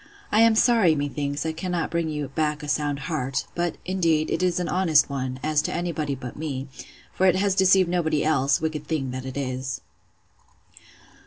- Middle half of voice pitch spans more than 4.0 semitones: No, average, 3.7 semitones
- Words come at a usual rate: Yes, average, 190 wpm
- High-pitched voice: No, medium, 155 Hz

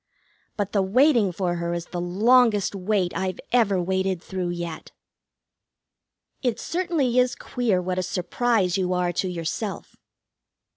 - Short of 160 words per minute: Yes, average, 140 wpm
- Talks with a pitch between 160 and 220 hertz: Yes, high, 190 Hz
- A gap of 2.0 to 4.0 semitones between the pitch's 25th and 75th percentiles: No, average, 4.4 semitones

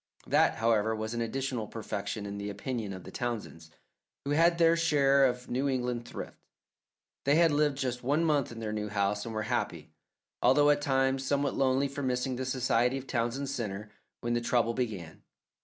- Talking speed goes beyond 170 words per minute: Yes, average, 190 wpm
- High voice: No, low, 125 Hz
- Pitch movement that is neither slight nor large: Yes, average, 3.8 semitones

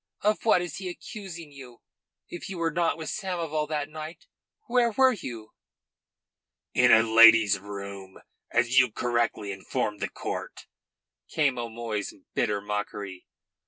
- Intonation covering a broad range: Yes, wide, 7.9 semitones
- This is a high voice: No, low, 130 Hz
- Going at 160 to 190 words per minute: No, slow, 135 wpm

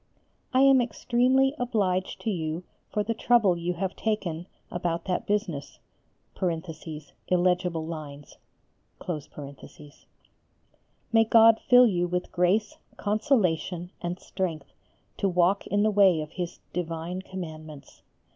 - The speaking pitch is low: No, medium, 185 Hz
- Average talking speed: No, slow, 115 wpm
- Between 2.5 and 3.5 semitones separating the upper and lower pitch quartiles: No, average, 4.1 semitones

